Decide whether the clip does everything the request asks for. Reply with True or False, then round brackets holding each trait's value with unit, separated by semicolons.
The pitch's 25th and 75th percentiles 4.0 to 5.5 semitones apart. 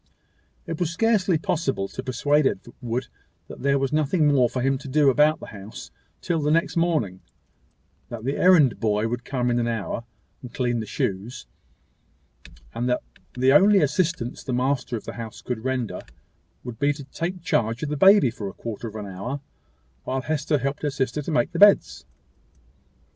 True (4.5 semitones)